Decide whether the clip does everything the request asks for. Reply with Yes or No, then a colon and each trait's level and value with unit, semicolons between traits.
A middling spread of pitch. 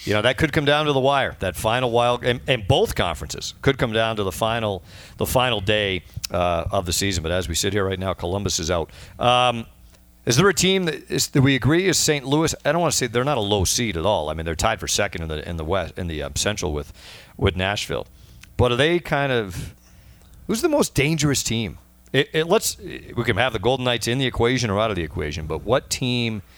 No: wide, 6.4 semitones